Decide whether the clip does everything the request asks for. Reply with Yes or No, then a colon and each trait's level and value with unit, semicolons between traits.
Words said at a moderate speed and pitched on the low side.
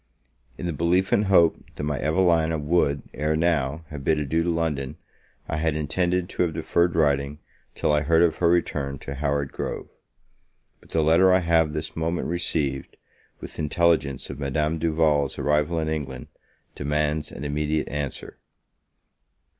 Yes: average, 160 wpm; very low, 80 Hz